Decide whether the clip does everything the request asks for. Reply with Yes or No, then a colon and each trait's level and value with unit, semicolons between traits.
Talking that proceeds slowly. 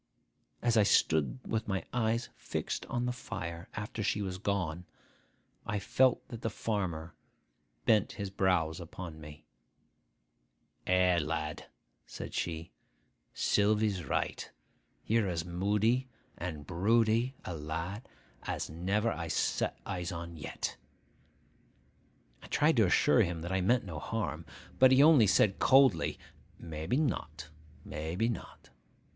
Yes: slow, 130 wpm